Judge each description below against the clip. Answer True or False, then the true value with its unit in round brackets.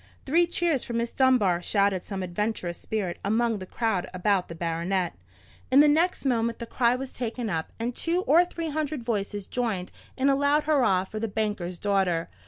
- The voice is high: True (225 Hz)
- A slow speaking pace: False (190 wpm)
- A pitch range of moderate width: False (6.0 semitones)